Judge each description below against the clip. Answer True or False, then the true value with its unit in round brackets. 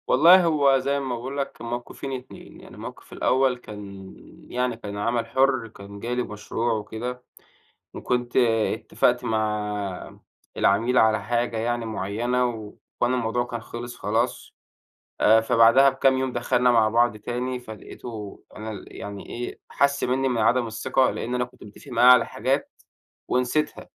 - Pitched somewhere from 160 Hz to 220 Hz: False (120 Hz)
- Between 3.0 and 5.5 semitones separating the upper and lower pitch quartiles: False (2.4 semitones)